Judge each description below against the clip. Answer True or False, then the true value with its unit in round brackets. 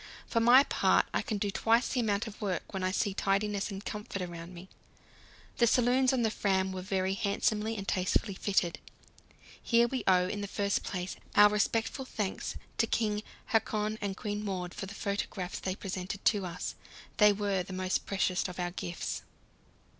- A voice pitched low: False (200 Hz)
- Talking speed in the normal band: True (185 wpm)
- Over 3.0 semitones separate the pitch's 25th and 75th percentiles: False (2.4 semitones)